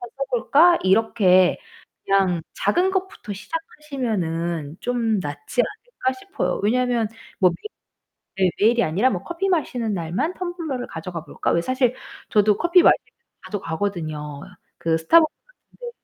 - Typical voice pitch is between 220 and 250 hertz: Yes, high, 225 Hz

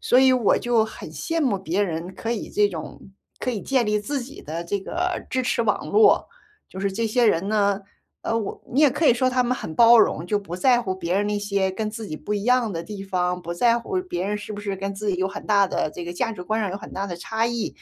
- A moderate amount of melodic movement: Yes, average, 4.0 semitones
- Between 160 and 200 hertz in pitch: No, high, 210 Hz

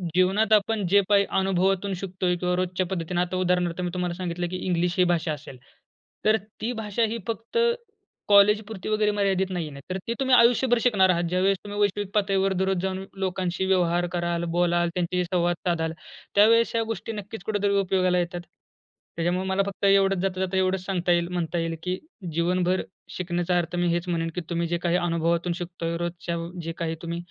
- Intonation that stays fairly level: Yes, narrow, 2.2 semitones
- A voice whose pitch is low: No, medium, 185 Hz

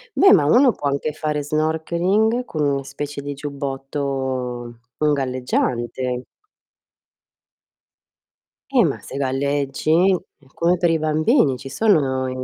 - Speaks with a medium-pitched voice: Yes, medium, 145 Hz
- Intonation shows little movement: No, average, 3.1 semitones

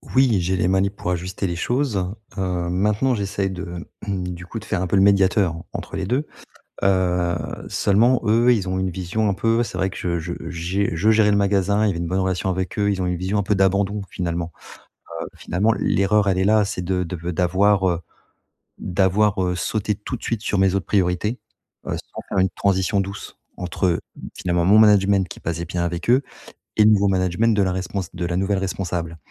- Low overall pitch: Yes, very low, 95 Hz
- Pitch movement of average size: No, narrow, 2.3 semitones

